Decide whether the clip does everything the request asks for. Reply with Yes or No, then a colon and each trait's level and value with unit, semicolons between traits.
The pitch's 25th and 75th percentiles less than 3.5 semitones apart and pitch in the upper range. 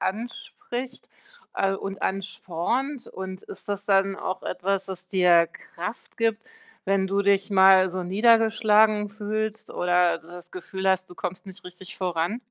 Yes: narrow, 2.5 semitones; high, 195 Hz